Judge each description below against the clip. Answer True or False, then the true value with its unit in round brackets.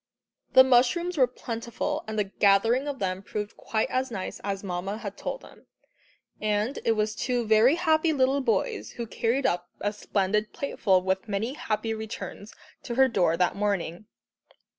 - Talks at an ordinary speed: True (165 wpm)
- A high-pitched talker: True (220 Hz)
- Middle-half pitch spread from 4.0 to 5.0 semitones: True (4.5 semitones)